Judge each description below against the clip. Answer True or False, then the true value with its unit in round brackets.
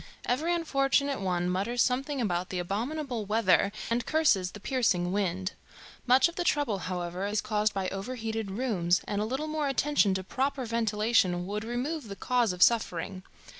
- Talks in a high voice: True (220 Hz)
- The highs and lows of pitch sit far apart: True (5.7 semitones)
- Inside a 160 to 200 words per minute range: True (170 wpm)